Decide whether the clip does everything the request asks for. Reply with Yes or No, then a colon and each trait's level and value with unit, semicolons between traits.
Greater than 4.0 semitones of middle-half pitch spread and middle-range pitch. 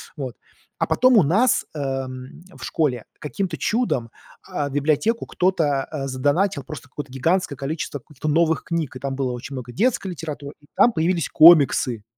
Yes: average, 4.4 semitones; medium, 145 Hz